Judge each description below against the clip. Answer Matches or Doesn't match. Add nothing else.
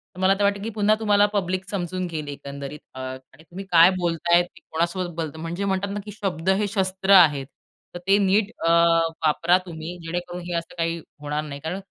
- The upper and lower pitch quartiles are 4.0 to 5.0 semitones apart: Doesn't match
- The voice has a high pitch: Doesn't match